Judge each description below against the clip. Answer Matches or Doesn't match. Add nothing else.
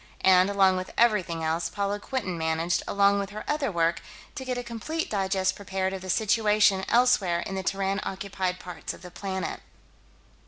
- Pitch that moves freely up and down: Doesn't match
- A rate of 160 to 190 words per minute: Matches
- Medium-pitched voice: Doesn't match